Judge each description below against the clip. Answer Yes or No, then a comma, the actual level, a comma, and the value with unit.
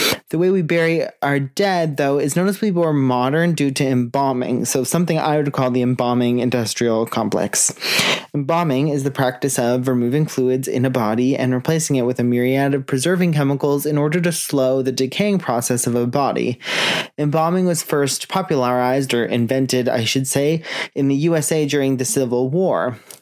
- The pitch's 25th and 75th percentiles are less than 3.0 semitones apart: No, average, 3.8 semitones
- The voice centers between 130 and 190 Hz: Yes, medium, 140 Hz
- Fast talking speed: No, average, 180 wpm